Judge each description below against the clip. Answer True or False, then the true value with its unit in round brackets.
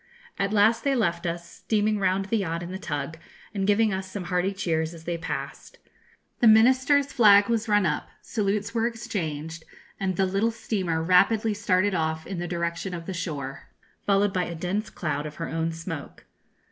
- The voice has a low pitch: False (190 Hz)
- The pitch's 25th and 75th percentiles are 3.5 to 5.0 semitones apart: True (4.0 semitones)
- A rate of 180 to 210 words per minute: True (185 wpm)